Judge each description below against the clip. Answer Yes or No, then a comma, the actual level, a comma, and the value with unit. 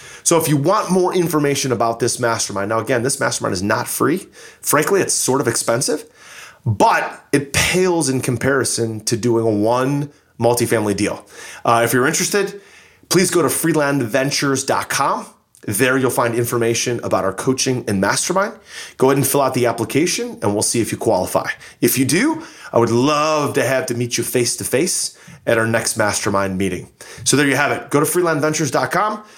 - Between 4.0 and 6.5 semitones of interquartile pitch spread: Yes, average, 4.4 semitones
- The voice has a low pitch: Yes, low, 130 Hz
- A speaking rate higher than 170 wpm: Yes, average, 180 wpm